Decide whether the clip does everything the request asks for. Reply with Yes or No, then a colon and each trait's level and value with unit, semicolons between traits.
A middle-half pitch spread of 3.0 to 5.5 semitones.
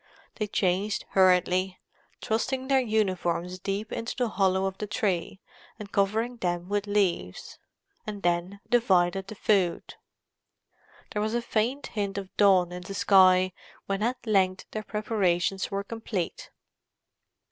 No: narrow, 2.6 semitones